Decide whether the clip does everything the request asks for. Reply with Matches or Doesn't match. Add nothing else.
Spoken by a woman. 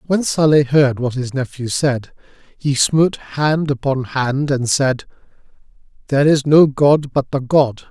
Doesn't match